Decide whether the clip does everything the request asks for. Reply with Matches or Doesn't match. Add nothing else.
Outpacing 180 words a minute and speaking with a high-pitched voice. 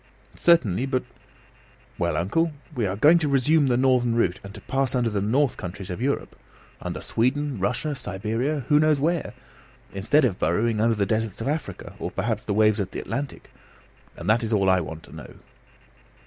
Doesn't match